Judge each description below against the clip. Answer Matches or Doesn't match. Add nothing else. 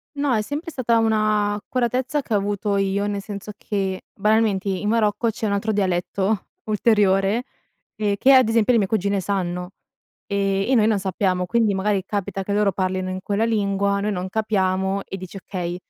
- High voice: Matches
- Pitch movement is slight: Matches